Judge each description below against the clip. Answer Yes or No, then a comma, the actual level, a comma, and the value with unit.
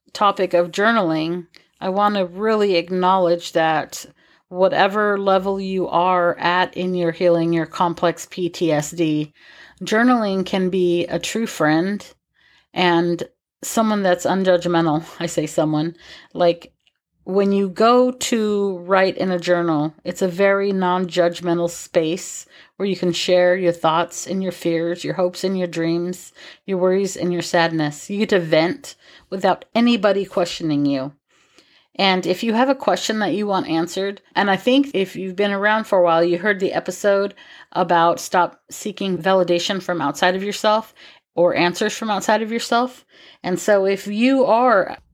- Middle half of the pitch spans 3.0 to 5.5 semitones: No, narrow, 2.6 semitones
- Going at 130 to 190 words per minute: Yes, average, 155 wpm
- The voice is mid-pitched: Yes, medium, 180 Hz